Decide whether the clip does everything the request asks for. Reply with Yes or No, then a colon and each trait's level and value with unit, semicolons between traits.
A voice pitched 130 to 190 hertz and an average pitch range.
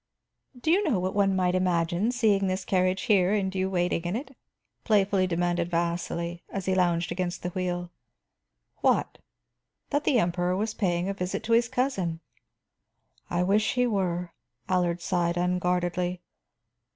No: medium, 185 Hz; narrow, 2.2 semitones